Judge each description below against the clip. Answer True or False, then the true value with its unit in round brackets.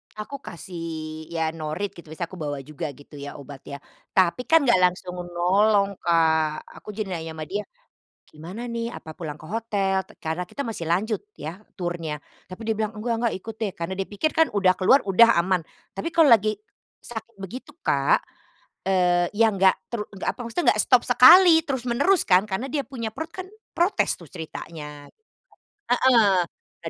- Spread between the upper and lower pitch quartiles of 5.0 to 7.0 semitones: True (5.4 semitones)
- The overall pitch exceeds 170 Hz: True (190 Hz)